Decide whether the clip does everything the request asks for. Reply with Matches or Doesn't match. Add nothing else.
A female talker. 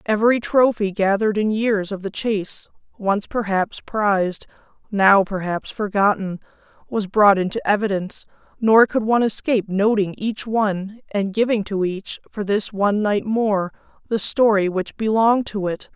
Matches